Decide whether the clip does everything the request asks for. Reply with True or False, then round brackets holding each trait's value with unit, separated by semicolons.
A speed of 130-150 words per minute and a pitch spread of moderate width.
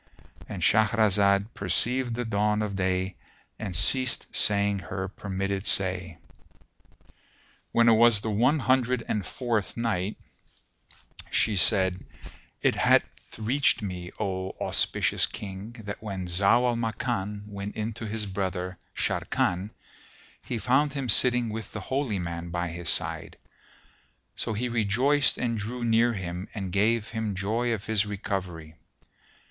True (135 wpm; 3.5 semitones)